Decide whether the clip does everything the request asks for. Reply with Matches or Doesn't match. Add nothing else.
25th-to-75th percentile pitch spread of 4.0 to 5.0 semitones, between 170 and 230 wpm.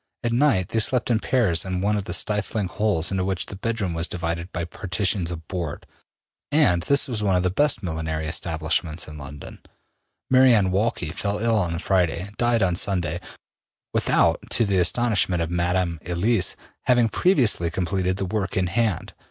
Matches